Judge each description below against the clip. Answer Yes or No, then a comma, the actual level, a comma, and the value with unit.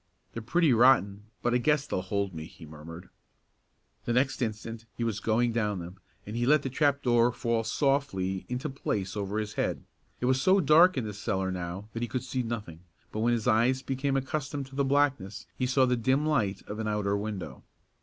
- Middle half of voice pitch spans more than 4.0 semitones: Yes, average, 4.5 semitones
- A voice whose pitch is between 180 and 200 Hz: No, low, 115 Hz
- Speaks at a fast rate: Yes, fast, 210 wpm